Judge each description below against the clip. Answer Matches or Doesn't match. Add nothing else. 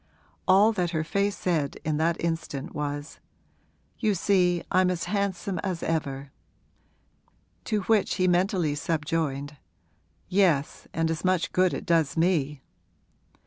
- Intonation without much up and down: Doesn't match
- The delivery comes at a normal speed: Doesn't match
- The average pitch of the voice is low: Doesn't match